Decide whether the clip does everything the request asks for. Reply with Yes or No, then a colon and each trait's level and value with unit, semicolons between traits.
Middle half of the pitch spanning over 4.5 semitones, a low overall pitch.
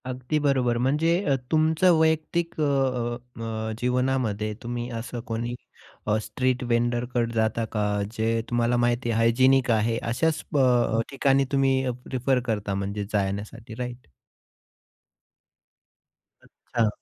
No: average, 2.8 semitones; low, 120 Hz